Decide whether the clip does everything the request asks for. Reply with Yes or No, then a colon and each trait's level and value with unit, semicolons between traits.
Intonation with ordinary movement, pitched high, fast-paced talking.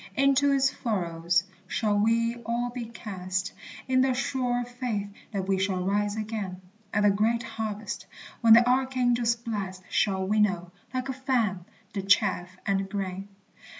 No: average, 3.9 semitones; high, 215 Hz; average, 150 wpm